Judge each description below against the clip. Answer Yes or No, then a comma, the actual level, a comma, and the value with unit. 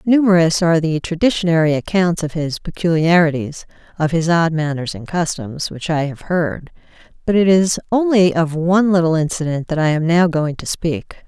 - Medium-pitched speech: Yes, medium, 165 Hz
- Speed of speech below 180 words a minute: Yes, average, 165 wpm